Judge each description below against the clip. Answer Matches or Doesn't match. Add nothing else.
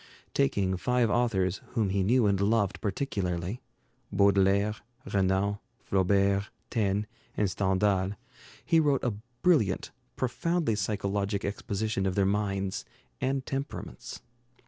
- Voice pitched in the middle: Doesn't match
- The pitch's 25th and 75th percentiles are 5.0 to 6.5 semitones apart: Doesn't match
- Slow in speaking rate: Matches